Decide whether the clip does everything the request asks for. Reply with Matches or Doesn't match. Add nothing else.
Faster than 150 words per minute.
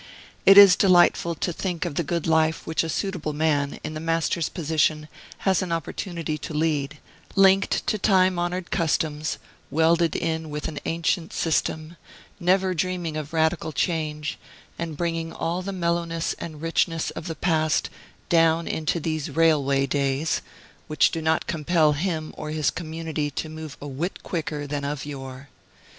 Matches